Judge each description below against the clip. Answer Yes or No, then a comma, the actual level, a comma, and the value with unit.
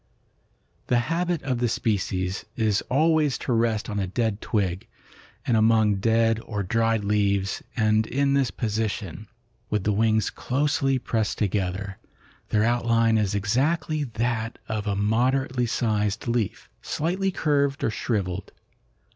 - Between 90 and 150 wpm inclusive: Yes, slow, 135 wpm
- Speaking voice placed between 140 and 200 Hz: No, low, 115 Hz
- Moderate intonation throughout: Yes, average, 3.3 semitones